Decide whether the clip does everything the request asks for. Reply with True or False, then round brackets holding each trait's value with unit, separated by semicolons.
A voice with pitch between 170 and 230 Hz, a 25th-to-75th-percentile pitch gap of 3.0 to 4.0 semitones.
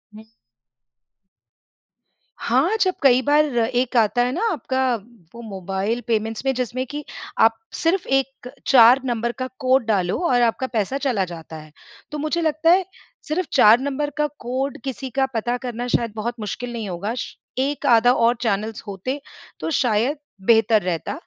False (245 Hz; 3.5 semitones)